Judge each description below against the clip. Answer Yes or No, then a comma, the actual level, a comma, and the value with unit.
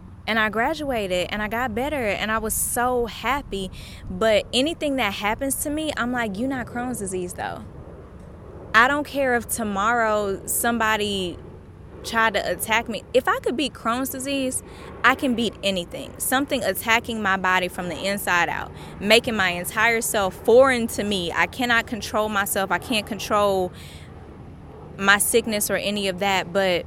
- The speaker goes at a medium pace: Yes, average, 165 wpm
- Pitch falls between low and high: No, high, 220 Hz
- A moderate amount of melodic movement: Yes, average, 4.1 semitones